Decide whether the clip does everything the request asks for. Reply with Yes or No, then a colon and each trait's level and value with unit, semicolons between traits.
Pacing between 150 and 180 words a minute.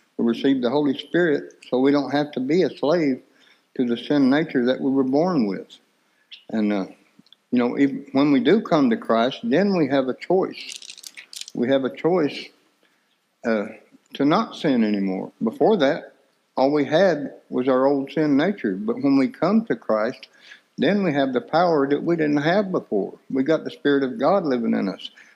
No: average, 195 wpm